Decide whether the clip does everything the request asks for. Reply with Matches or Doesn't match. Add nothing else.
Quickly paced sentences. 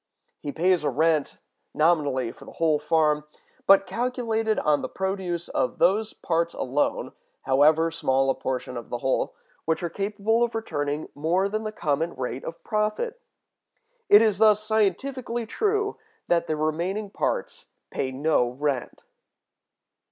Doesn't match